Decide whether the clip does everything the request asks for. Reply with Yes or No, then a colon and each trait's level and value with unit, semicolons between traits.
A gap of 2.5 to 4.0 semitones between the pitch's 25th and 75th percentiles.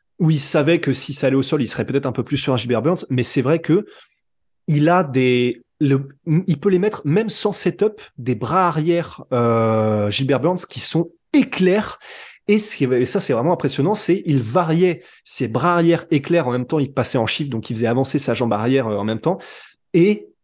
No: wide, 5.5 semitones